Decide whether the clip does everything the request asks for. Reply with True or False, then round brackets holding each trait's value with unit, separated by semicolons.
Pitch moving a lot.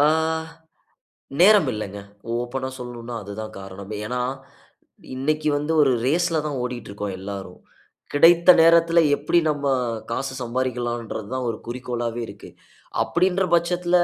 True (5.8 semitones)